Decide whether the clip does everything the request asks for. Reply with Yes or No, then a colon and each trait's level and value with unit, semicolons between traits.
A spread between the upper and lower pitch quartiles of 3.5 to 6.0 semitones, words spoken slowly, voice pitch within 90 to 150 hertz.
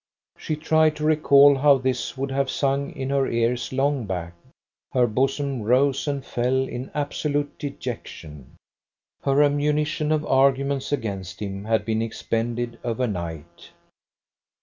Yes: average, 3.8 semitones; slow, 130 wpm; low, 135 Hz